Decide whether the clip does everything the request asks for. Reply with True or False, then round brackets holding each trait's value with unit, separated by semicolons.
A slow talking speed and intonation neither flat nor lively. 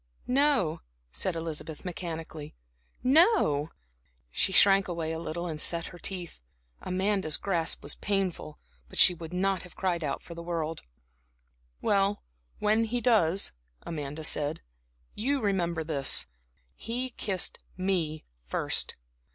True (120 wpm; 3.7 semitones)